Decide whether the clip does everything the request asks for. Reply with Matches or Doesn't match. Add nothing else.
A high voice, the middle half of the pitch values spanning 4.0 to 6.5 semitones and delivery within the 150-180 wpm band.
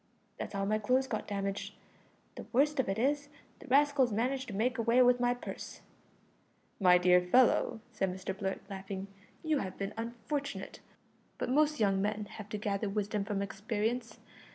Matches